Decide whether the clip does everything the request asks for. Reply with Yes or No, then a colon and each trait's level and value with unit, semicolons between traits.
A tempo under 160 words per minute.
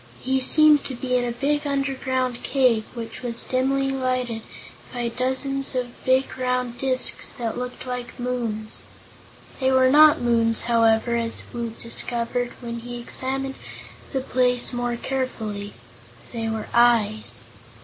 Yes: average, 140 wpm